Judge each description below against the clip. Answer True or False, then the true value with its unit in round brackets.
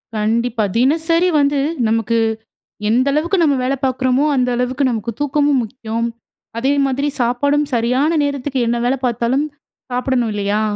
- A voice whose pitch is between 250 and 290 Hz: True (255 Hz)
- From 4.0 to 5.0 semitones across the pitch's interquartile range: False (3.3 semitones)